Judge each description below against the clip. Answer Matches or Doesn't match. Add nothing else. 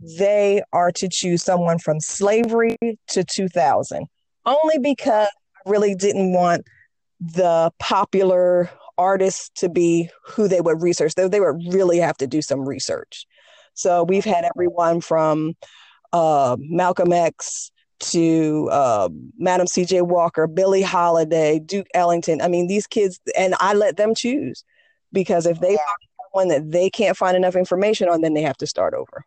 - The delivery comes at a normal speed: Matches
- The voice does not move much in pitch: Doesn't match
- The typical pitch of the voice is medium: Matches